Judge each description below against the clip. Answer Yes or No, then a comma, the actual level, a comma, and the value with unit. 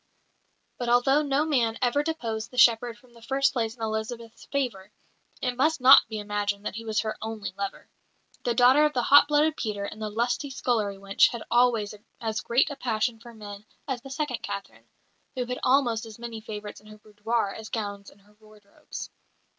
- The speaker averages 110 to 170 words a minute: No, average, 195 wpm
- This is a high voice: Yes, high, 230 Hz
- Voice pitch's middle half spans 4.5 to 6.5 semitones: No, average, 2.9 semitones